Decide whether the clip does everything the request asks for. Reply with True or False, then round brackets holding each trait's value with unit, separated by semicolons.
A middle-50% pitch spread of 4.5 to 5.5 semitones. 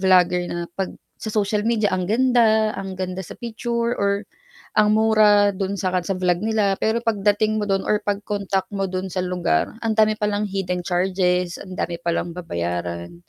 False (2.9 semitones)